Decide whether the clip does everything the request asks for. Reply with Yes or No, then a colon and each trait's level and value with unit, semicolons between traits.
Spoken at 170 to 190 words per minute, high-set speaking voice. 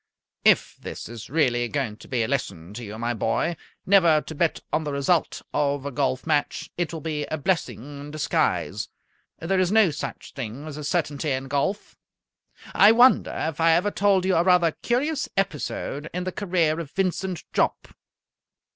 No: average, 180 wpm; medium, 155 Hz